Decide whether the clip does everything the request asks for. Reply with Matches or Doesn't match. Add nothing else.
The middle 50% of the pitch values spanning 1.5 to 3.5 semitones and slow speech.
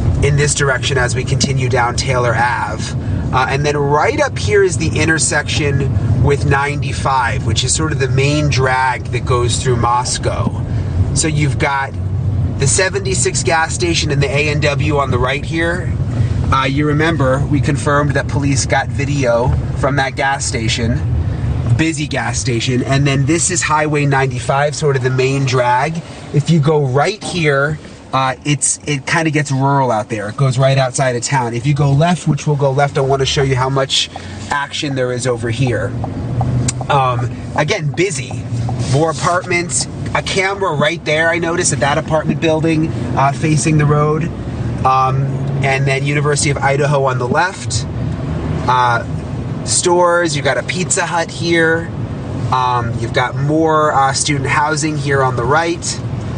Doesn't match